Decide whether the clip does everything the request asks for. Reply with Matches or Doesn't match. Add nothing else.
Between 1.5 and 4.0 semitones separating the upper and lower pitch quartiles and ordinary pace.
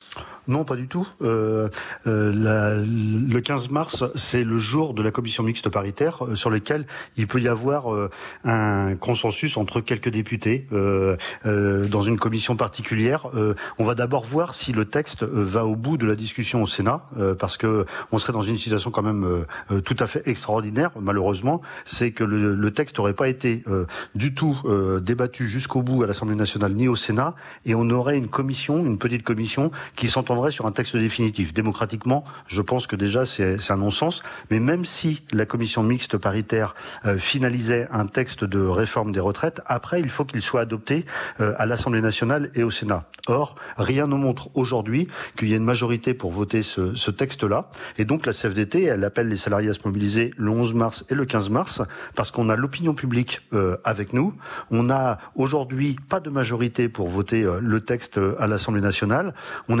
Matches